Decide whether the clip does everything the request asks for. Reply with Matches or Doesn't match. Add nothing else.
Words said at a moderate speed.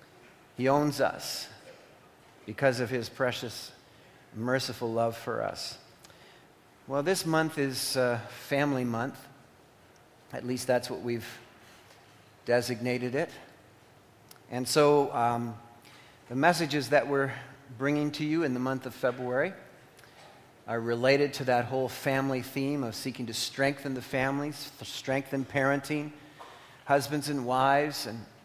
Doesn't match